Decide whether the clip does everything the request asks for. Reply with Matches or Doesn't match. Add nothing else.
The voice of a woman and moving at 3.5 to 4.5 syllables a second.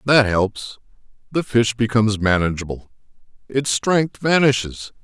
Doesn't match